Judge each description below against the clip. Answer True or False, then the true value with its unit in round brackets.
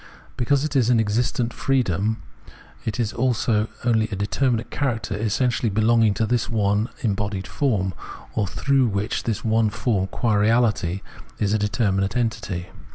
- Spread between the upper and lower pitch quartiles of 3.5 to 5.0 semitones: False (2.9 semitones)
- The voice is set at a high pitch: False (110 Hz)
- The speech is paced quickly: False (150 wpm)